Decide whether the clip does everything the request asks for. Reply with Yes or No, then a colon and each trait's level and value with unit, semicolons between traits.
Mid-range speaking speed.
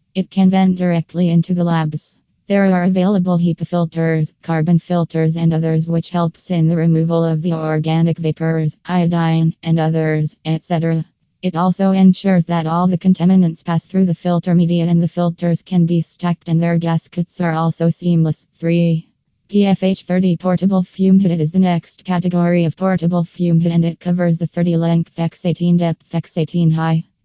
Yes: average, 175 wpm